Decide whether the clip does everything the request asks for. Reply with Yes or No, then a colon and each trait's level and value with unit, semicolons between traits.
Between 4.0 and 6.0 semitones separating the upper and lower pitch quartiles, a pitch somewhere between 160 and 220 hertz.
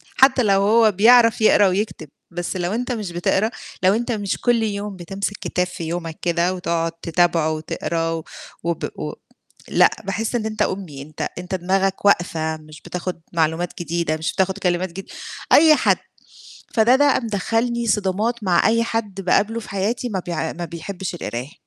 Yes: average, 4.4 semitones; high, 190 Hz